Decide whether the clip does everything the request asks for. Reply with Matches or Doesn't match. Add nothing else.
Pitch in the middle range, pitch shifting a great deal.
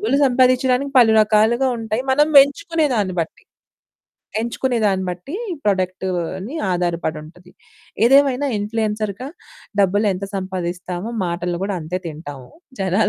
Doesn't match